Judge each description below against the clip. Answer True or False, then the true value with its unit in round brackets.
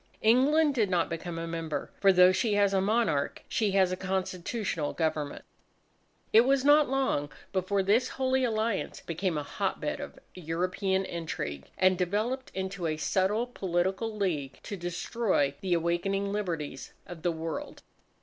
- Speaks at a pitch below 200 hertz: True (190 Hz)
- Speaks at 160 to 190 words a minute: False (150 wpm)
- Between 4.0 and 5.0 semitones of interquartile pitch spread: True (4.4 semitones)